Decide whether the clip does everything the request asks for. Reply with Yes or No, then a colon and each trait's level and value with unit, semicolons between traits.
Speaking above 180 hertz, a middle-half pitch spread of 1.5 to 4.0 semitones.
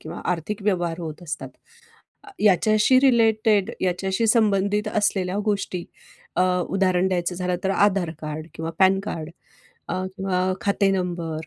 Yes: high, 190 Hz; average, 2.8 semitones